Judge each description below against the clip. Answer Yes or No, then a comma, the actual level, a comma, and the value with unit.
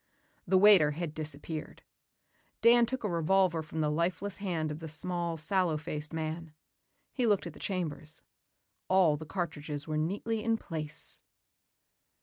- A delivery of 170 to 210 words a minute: No, average, 145 wpm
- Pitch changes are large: No, average, 3.6 semitones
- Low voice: No, medium, 165 Hz